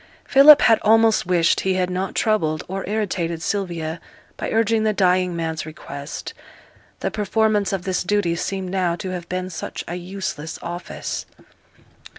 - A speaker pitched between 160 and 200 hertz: Yes, medium, 185 Hz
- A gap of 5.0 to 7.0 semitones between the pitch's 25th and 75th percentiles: No, average, 3.2 semitones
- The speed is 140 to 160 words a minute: Yes, average, 155 wpm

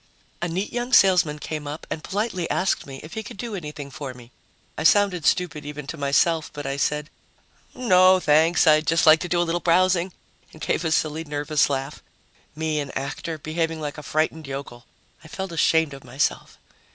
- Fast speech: No, average, 195 wpm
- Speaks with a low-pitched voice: No, medium, 160 Hz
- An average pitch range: Yes, average, 3.0 semitones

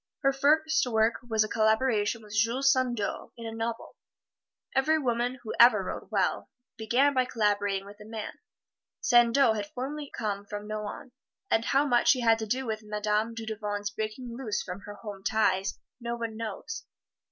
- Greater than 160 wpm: Yes, average, 170 wpm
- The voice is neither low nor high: No, high, 225 Hz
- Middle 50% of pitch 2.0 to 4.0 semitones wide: Yes, average, 3.0 semitones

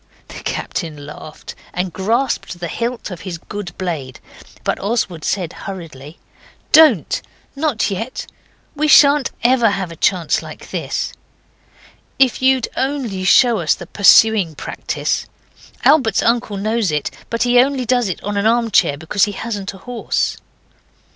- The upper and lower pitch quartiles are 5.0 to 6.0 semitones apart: Yes, wide, 5.6 semitones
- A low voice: No, high, 205 Hz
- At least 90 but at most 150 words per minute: Yes, average, 145 wpm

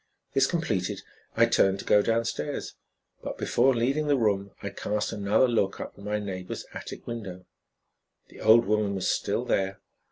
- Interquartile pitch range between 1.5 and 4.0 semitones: Yes, average, 3.1 semitones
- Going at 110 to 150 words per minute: No, average, 165 wpm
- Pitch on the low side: Yes, low, 105 Hz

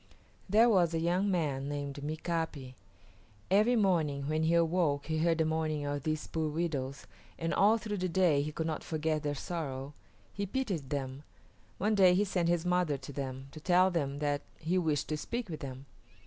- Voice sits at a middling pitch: Yes, medium, 160 Hz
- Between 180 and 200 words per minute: Yes, average, 190 wpm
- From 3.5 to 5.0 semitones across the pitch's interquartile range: Yes, average, 3.8 semitones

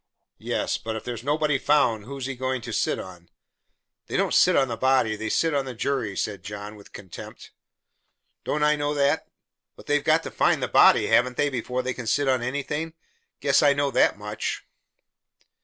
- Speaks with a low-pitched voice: Yes, low, 130 Hz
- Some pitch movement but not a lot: Yes, average, 4.4 semitones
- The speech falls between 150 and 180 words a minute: No, average, 195 wpm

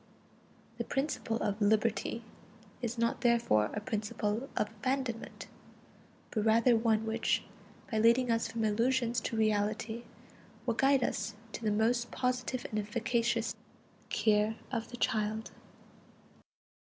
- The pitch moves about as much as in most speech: No, narrow, 1.8 semitones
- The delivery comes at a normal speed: No, slow, 125 wpm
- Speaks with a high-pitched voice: Yes, high, 230 Hz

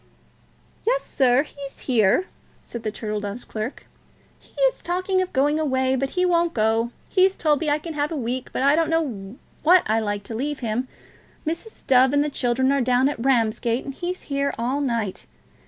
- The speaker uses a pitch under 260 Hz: No, very high, 270 Hz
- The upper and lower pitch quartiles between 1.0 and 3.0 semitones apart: No, average, 4.9 semitones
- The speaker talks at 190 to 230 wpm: Yes, average, 195 wpm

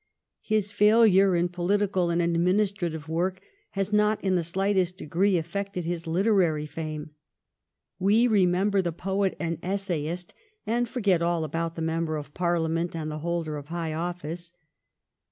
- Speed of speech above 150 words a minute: No, average, 145 wpm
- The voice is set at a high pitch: No, medium, 175 Hz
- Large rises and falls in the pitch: No, average, 3.0 semitones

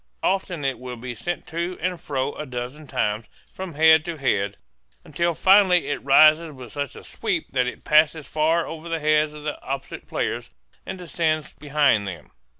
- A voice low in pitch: No, medium, 150 Hz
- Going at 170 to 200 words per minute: Yes, average, 180 wpm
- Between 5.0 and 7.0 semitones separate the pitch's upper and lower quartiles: No, average, 3.9 semitones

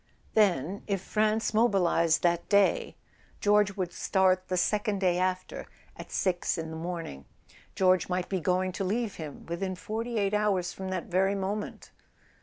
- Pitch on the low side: No, high, 190 Hz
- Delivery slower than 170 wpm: Yes, average, 160 wpm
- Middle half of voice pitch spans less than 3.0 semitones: Yes, narrow, 2.5 semitones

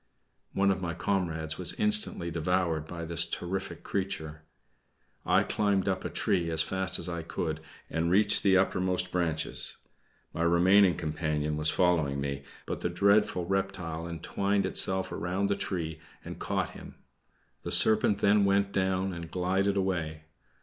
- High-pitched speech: No, very low, 90 Hz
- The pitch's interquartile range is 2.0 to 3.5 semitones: Yes, average, 2.9 semitones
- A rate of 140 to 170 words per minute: Yes, average, 150 wpm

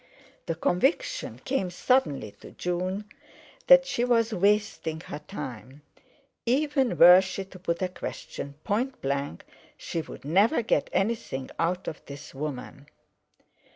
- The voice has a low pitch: No, medium, 185 Hz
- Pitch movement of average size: No, wide, 7.6 semitones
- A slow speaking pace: Yes, slow, 130 wpm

